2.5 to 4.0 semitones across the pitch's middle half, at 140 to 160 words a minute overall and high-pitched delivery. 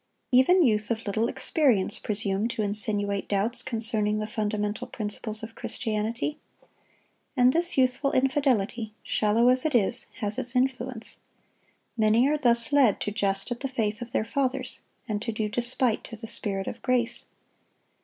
Yes: average, 3.1 semitones; average, 155 wpm; high, 230 Hz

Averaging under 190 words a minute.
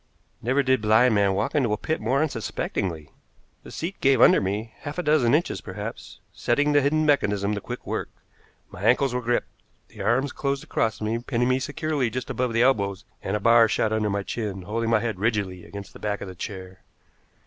No: fast, 205 wpm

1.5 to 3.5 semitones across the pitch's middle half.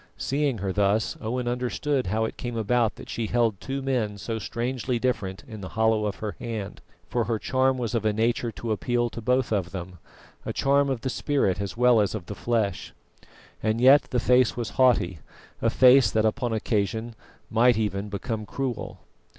Yes: average, 3.0 semitones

